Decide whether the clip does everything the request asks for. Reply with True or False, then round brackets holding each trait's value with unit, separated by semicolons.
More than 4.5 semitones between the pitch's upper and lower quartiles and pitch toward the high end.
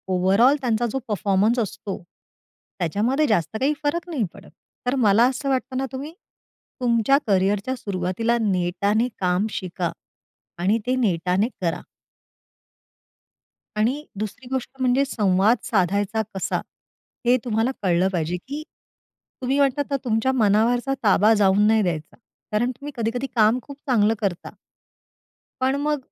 True (4.9 semitones; 225 Hz)